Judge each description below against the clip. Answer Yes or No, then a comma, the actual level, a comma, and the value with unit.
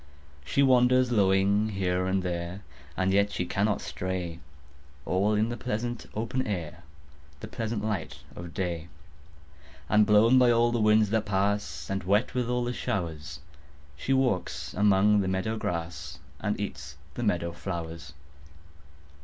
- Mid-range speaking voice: No, low, 100 Hz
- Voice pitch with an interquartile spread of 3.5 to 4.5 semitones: Yes, average, 4.1 semitones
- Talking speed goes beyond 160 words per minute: No, average, 145 wpm